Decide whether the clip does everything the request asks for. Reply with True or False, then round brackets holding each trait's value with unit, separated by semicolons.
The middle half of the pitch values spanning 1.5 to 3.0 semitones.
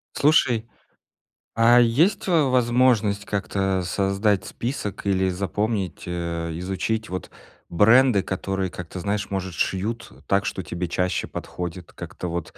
False (3.9 semitones)